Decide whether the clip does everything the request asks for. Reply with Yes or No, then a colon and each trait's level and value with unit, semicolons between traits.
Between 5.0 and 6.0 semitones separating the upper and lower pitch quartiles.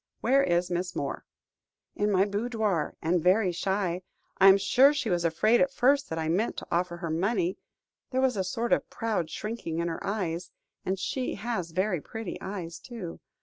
No: average, 4.5 semitones